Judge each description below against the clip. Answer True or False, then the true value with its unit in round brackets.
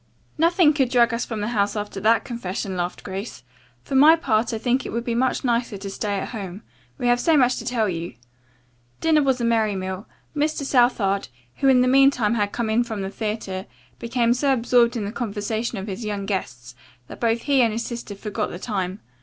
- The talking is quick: True (215 wpm)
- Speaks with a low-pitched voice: False (230 Hz)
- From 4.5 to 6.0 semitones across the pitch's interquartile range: False (3.6 semitones)